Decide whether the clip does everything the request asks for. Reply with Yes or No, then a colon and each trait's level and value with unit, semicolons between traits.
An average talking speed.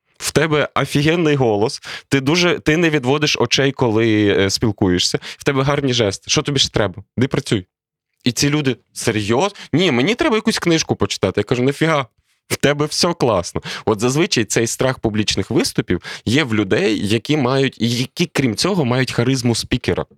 No: fast, 165 wpm